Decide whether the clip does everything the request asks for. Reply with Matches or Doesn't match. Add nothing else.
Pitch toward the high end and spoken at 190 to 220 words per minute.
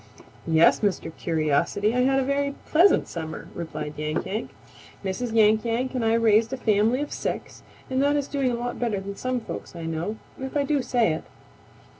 Matches